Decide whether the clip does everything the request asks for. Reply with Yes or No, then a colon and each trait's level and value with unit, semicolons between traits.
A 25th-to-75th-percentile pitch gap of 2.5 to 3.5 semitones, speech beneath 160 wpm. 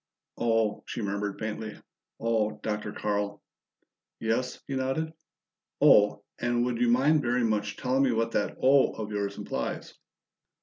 Yes: average, 3.1 semitones; average, 140 wpm